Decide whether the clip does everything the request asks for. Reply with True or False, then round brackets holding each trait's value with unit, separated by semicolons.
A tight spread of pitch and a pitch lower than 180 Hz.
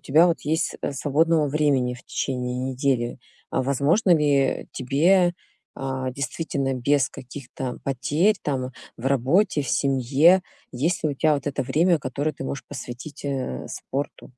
False (3.0 semitones; 140 Hz)